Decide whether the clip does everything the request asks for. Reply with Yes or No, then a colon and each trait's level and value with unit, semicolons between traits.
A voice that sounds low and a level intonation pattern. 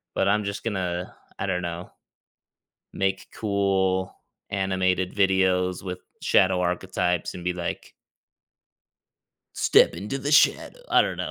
Yes: very low, 95 Hz; narrow, 1.3 semitones